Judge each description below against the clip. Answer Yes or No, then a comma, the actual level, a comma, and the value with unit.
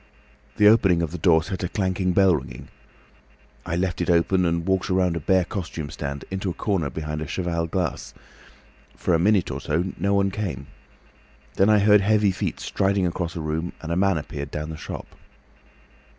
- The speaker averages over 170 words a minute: Yes, average, 195 wpm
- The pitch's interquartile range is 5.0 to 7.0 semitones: No, average, 3.2 semitones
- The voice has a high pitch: No, very low, 90 Hz